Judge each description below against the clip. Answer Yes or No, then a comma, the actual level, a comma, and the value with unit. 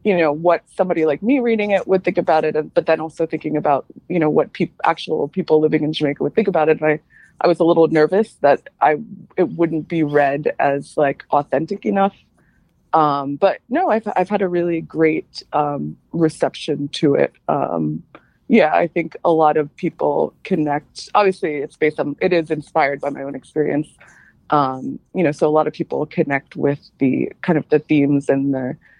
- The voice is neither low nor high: Yes, medium, 155 Hz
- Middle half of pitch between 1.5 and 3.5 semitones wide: Yes, average, 3.2 semitones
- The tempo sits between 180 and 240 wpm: Yes, average, 200 wpm